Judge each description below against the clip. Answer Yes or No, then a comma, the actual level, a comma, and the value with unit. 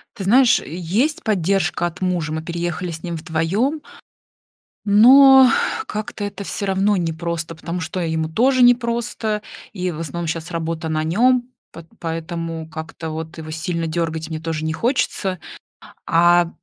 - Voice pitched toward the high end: No, medium, 175 Hz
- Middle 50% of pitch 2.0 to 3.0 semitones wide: No, average, 4.4 semitones